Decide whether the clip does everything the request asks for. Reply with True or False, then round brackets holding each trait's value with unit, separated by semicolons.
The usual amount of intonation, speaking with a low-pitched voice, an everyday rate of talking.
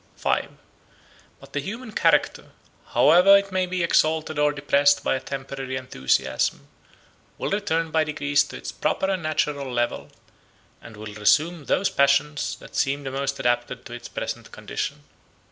False (3.6 semitones; 145 Hz; 155 wpm)